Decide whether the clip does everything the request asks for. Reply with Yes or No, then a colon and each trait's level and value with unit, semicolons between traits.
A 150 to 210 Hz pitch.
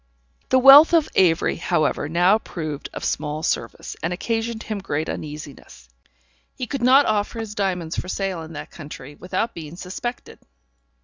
Yes: medium, 185 Hz